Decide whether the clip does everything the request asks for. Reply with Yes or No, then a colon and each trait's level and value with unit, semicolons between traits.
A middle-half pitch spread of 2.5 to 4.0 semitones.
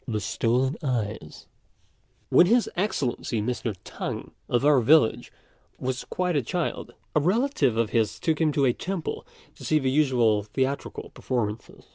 No: average, 5.2 semitones